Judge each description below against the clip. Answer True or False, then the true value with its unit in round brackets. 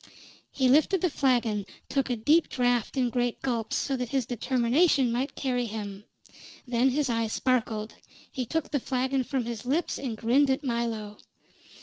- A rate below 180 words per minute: True (170 wpm)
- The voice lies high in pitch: True (250 Hz)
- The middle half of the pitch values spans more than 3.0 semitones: False (2.6 semitones)